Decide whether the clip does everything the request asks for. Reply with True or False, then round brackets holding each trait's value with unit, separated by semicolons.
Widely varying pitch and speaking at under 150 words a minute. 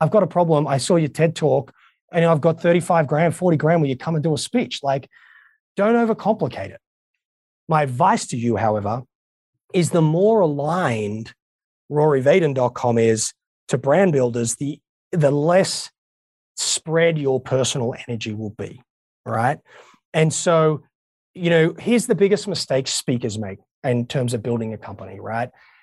False (6.1 semitones; 160 wpm)